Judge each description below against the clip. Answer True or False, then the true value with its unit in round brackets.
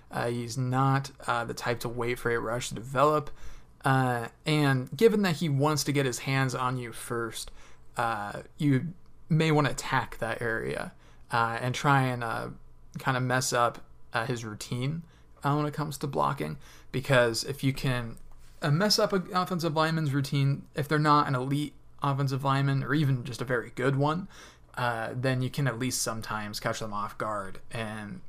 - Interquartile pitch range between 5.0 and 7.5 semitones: False (3.7 semitones)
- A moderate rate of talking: True (190 wpm)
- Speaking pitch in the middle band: False (130 Hz)